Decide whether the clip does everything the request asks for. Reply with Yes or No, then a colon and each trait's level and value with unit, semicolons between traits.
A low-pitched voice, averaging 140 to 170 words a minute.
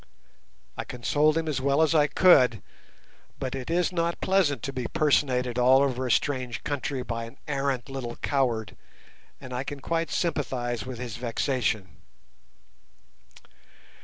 Yes: low, 130 Hz; average, 145 wpm